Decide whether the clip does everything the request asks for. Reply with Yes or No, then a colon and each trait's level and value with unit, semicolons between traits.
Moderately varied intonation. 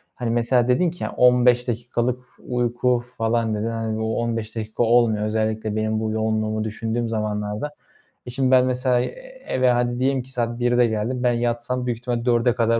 No: narrow, 2.0 semitones